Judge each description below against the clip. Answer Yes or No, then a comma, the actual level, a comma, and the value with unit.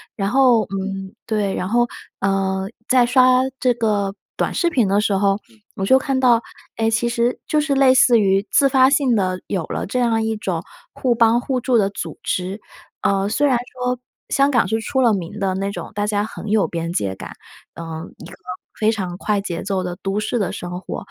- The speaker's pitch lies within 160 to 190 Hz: No, high, 215 Hz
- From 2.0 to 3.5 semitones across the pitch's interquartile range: No, average, 4.2 semitones